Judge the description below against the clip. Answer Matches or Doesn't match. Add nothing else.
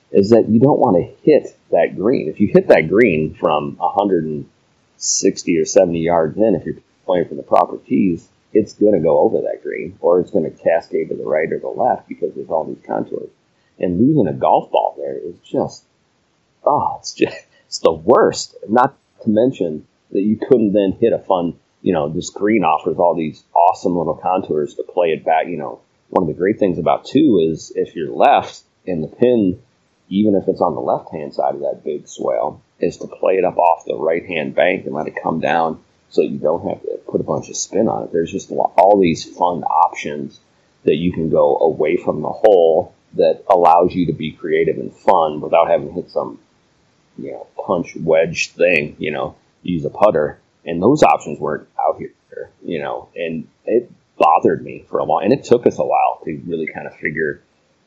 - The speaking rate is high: Matches